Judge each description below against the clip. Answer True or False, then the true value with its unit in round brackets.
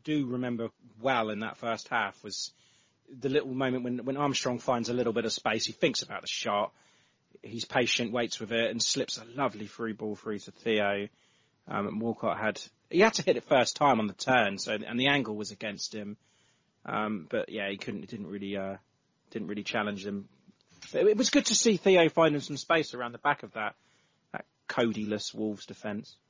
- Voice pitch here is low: True (115 Hz)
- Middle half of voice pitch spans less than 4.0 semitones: False (4.3 semitones)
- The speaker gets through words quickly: True (210 wpm)